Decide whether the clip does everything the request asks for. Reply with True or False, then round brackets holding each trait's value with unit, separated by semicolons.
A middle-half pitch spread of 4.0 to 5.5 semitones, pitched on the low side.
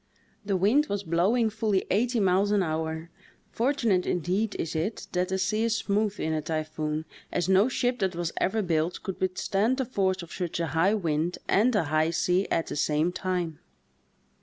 False (4.3 semitones; 185 Hz)